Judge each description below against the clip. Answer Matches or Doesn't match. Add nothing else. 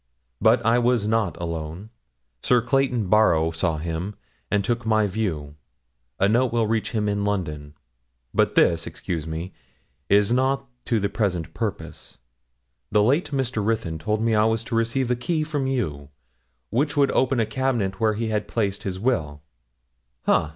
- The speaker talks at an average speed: Matches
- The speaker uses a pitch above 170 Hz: Doesn't match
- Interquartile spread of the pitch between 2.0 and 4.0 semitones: Doesn't match